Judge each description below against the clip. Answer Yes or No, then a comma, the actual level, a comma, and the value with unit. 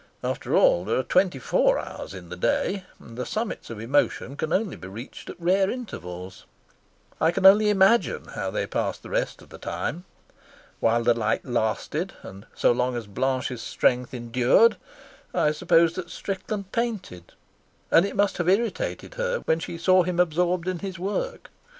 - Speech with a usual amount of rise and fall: No, wide, 8.4 semitones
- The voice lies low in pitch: No, medium, 170 Hz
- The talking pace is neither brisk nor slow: Yes, average, 175 wpm